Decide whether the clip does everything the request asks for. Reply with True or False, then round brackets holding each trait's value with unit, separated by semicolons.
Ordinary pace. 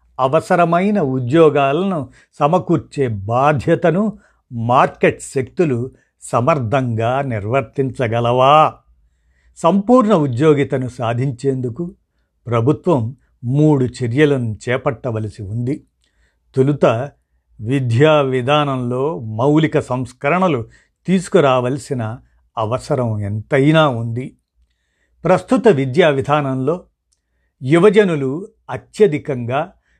False (60 wpm)